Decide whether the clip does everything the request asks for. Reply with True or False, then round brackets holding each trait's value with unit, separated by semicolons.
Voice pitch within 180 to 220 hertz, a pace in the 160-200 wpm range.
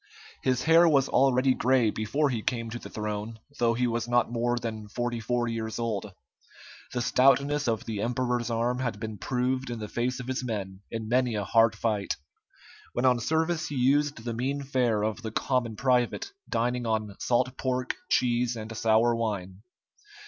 False (120 Hz; 180 wpm)